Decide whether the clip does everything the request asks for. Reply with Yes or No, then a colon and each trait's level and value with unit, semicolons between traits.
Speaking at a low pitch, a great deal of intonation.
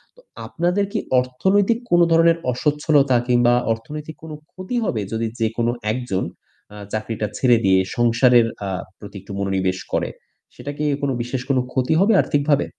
Yes: low, 130 Hz; wide, 5.9 semitones